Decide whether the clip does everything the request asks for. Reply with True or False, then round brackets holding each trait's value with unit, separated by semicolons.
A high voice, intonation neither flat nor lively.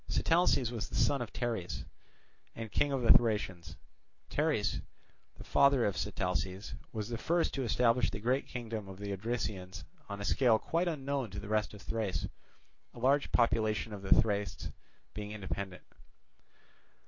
False (110 Hz; 3.6 semitones)